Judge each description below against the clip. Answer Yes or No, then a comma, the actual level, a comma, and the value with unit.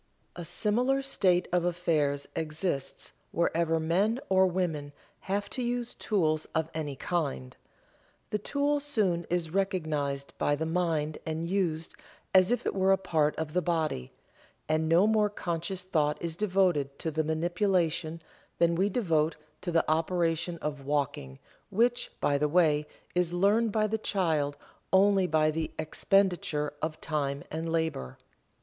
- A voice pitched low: No, medium, 170 Hz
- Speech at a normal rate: Yes, average, 150 wpm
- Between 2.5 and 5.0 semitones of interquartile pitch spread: Yes, average, 3.7 semitones